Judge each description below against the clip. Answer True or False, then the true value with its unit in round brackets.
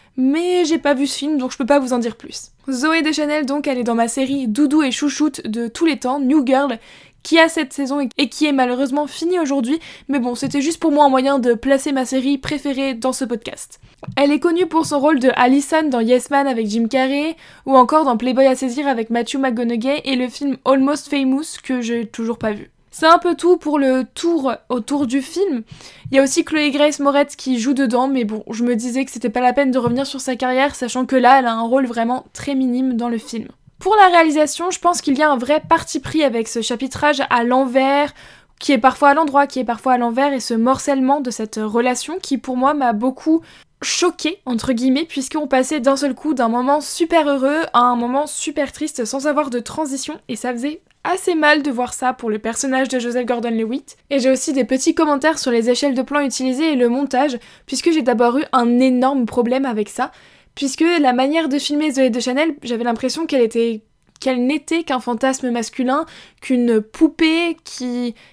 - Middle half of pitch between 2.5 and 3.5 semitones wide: True (3.0 semitones)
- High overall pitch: True (270 Hz)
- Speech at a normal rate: False (225 wpm)